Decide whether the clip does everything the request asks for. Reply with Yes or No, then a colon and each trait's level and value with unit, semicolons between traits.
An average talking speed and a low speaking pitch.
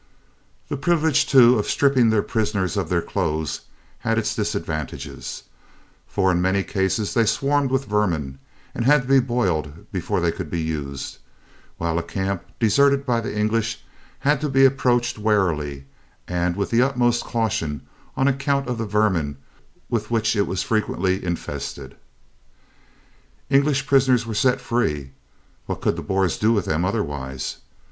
Yes: average, 155 wpm; low, 105 Hz